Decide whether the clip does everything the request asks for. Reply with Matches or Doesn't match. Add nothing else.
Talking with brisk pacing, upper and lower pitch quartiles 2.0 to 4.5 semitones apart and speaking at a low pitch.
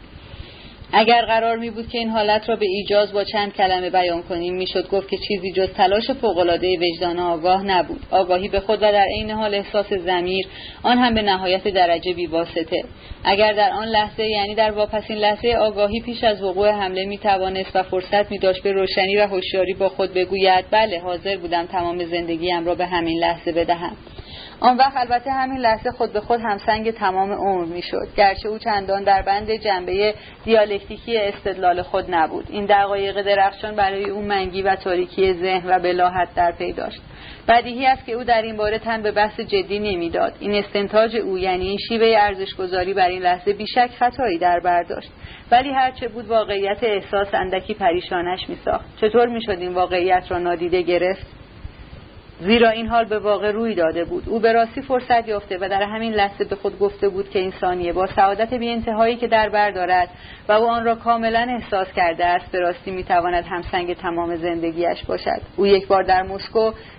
Doesn't match